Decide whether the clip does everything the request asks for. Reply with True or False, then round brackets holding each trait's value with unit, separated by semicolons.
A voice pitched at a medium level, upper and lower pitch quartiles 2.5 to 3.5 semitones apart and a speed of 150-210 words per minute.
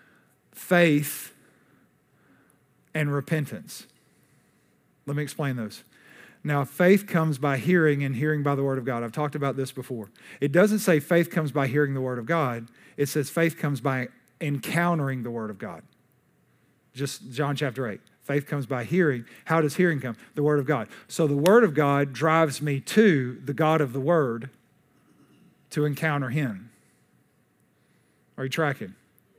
True (145 Hz; 2.9 semitones; 165 wpm)